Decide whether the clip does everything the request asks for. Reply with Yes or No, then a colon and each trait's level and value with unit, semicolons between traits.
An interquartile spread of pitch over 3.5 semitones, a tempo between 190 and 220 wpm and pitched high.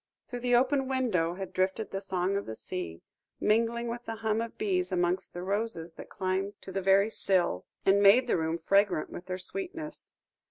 Yes: average, 4.1 semitones; average, 195 wpm; high, 195 Hz